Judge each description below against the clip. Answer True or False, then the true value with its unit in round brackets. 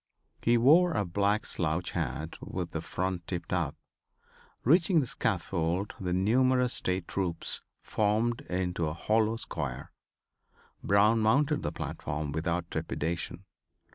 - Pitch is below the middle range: True (95 Hz)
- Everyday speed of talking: False (125 wpm)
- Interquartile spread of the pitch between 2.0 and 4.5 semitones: False (5.2 semitones)